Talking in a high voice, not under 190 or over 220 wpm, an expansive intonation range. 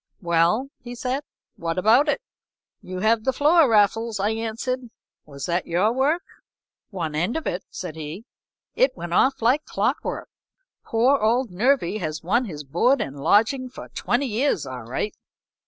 No: high, 220 Hz; average, 165 wpm; wide, 6.9 semitones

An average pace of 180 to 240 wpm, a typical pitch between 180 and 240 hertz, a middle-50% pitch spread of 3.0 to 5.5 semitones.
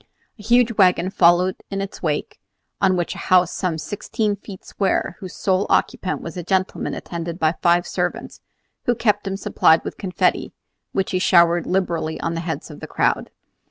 No: average, 185 wpm; medium, 185 Hz; narrow, 2.4 semitones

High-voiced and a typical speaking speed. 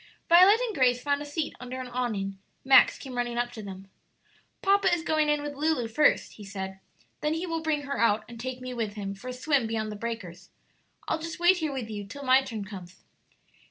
No: very high, 255 Hz; fast, 225 wpm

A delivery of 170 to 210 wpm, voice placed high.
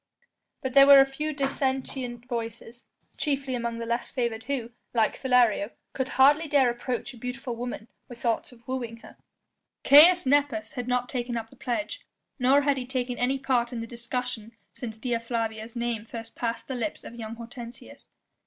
Yes: average, 180 wpm; high, 245 Hz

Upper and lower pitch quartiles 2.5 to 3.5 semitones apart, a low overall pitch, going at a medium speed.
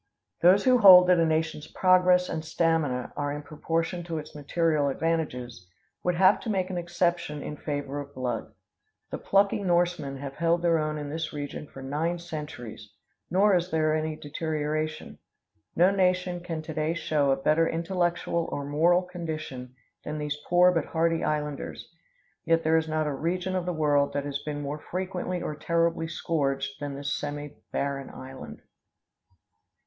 No: average, 3.2 semitones; medium, 160 Hz; average, 165 wpm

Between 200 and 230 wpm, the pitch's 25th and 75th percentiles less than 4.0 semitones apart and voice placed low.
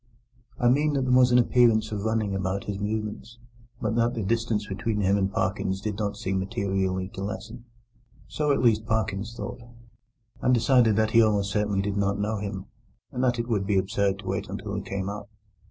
Yes: fast, 205 wpm; average, 2.8 semitones; low, 105 Hz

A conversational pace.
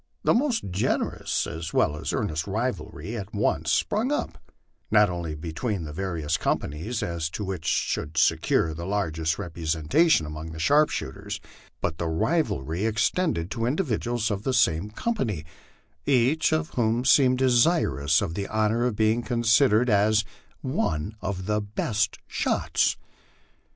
Yes: average, 150 wpm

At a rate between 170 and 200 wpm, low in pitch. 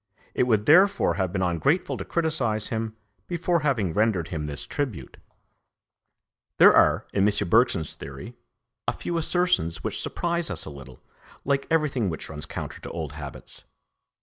No: average, 155 wpm; low, 110 Hz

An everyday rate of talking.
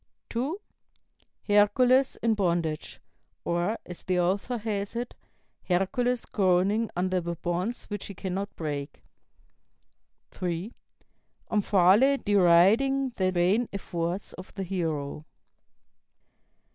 No: slow, 100 wpm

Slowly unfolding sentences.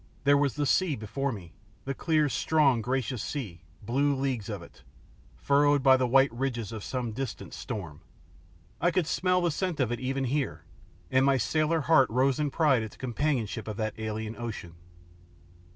No: average, 180 wpm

